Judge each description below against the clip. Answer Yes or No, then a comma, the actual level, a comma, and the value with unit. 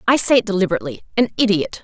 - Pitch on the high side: Yes, high, 195 Hz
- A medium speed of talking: Yes, average, 165 wpm